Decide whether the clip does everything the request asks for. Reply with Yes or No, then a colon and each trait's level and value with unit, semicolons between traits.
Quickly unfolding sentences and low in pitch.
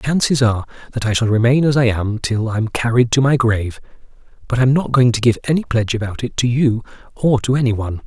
Yes: fast, 240 wpm; low, 120 Hz